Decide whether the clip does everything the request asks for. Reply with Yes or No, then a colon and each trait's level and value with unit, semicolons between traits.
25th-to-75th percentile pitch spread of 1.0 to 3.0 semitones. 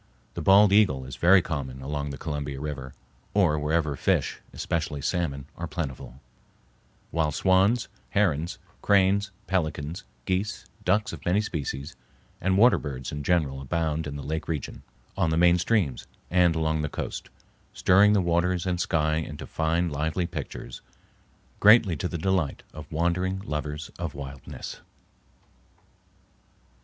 No: average, 4.0 semitones